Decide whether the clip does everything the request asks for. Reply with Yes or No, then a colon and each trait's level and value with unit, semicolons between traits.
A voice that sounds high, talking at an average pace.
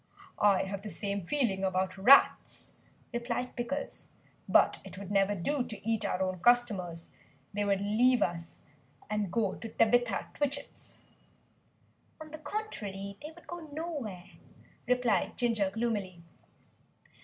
No: high, 215 Hz; slow, 130 wpm